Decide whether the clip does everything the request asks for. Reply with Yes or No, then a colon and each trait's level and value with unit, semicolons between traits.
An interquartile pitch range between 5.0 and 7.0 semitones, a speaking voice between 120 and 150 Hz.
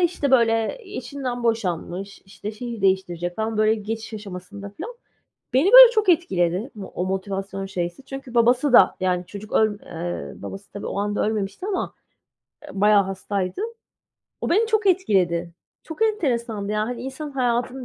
No: wide, 5.4 semitones; high, 220 Hz